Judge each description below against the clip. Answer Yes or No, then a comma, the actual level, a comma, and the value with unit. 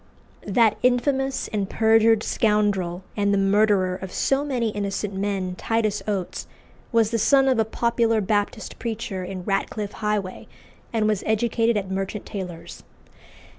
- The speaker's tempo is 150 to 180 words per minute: No, average, 140 wpm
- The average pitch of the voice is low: No, high, 210 Hz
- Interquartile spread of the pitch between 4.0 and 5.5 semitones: No, average, 2.7 semitones